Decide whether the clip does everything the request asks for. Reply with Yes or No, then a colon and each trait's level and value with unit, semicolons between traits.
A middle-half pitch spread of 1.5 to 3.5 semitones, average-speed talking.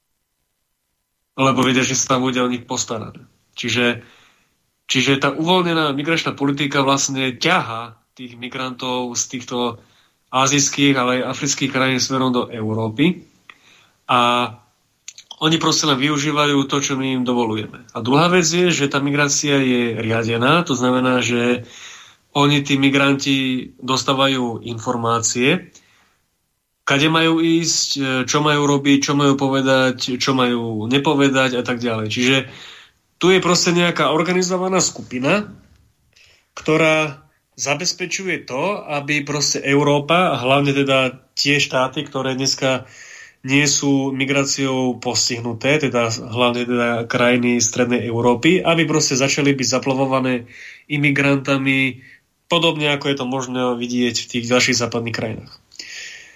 Yes: average, 2.9 semitones; average, 125 wpm